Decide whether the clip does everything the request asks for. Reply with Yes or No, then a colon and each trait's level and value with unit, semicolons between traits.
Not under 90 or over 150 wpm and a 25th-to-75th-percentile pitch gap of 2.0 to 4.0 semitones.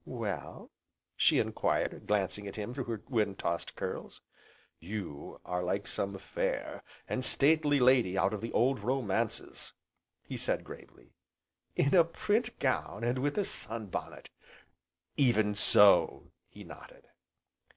No: slow, 135 wpm; average, 5.0 semitones